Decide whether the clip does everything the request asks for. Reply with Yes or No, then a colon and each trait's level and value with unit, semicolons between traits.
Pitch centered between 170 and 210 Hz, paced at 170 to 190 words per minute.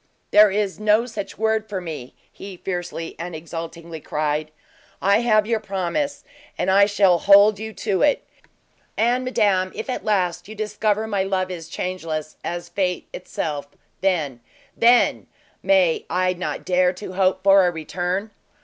No: high, 190 Hz; average, 155 wpm